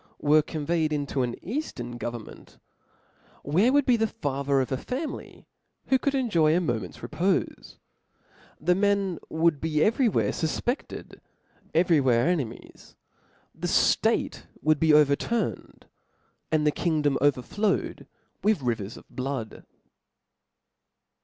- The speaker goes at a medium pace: No, slow, 120 wpm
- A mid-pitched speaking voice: Yes, medium, 155 Hz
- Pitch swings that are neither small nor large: No, wide, 6.2 semitones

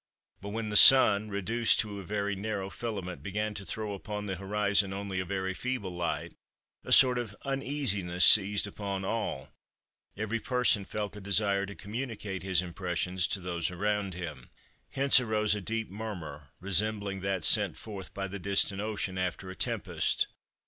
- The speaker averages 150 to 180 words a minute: Yes, average, 165 wpm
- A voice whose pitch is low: Yes, low, 100 Hz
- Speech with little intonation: Yes, narrow, 2.2 semitones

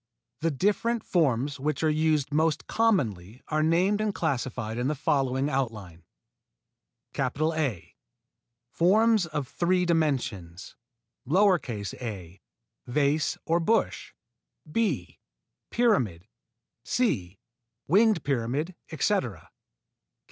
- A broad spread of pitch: Yes, wide, 6.3 semitones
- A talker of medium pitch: Yes, medium, 150 Hz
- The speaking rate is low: Yes, slow, 95 wpm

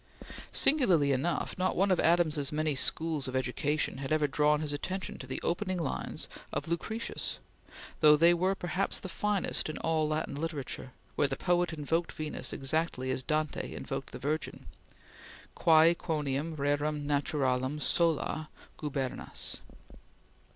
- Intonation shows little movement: No, average, 3.0 semitones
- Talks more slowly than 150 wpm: Yes, average, 140 wpm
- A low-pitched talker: No, medium, 155 Hz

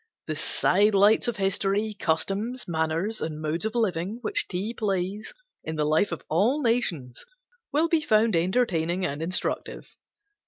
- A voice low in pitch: No, high, 195 Hz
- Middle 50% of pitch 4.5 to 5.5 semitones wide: Yes, average, 5.2 semitones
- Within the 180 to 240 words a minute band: No, average, 150 wpm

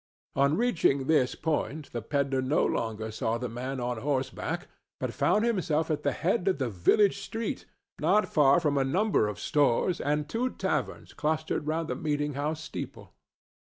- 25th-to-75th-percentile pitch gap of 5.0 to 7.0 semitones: No, average, 3.7 semitones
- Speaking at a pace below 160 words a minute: No, average, 170 wpm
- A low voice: No, medium, 145 Hz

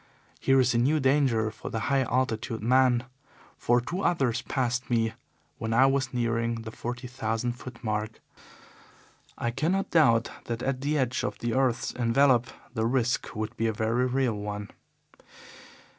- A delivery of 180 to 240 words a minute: No, average, 160 wpm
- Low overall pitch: Yes, low, 120 Hz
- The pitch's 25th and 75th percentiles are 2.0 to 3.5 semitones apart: Yes, narrow, 2.6 semitones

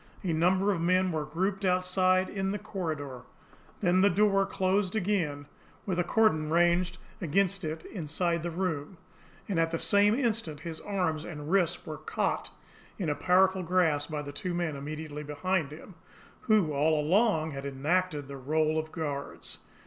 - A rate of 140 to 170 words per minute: Yes, average, 165 wpm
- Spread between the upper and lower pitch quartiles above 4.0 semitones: No, average, 3.5 semitones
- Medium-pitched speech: Yes, medium, 170 Hz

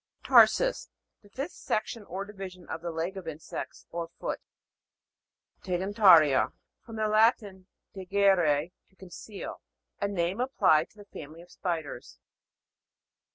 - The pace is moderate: No, slow, 130 wpm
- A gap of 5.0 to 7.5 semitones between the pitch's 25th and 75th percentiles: No, average, 3.5 semitones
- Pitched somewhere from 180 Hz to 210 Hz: Yes, high, 190 Hz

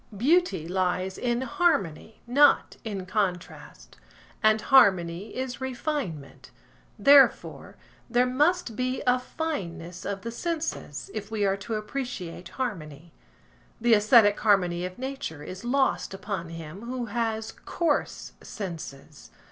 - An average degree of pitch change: No, wide, 6.0 semitones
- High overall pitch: Yes, high, 220 Hz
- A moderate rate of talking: No, slow, 120 wpm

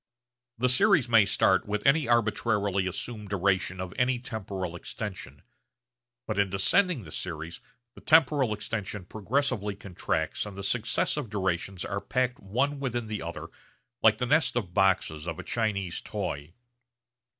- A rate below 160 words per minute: Yes, average, 145 wpm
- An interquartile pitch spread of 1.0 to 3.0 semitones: No, average, 4.5 semitones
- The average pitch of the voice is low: Yes, low, 105 Hz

